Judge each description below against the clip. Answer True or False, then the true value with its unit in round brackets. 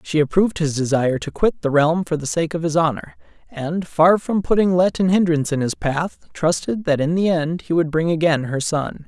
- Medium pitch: True (165 Hz)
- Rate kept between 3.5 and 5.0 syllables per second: False (5.3 syllables/s)